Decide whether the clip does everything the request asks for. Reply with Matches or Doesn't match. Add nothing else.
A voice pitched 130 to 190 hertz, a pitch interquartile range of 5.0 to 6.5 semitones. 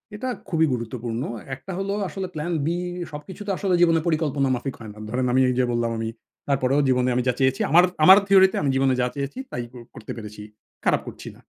Matches